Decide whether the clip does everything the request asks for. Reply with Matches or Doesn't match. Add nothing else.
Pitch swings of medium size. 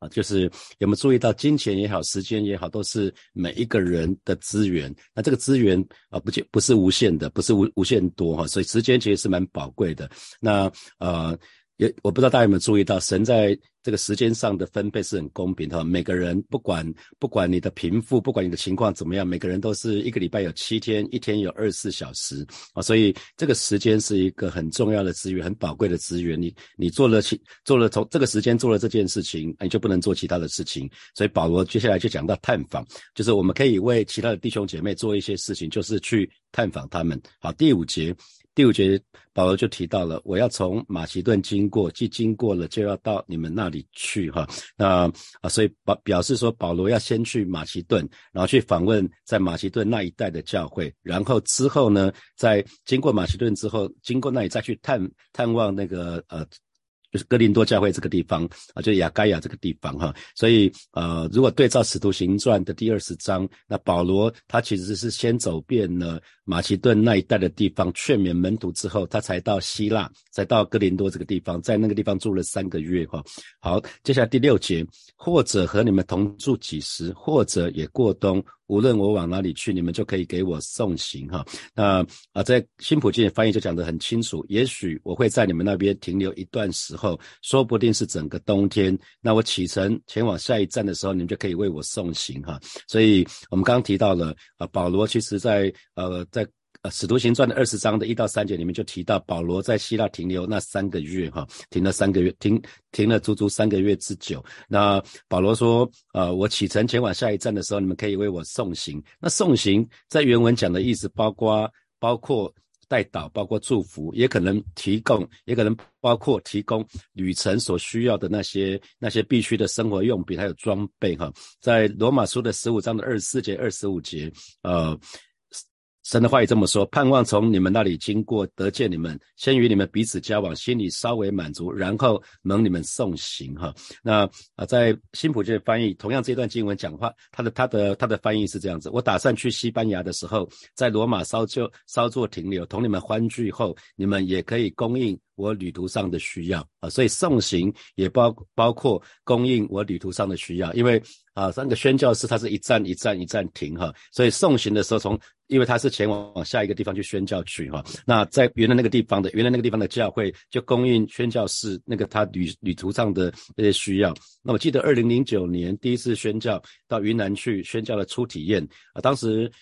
Matches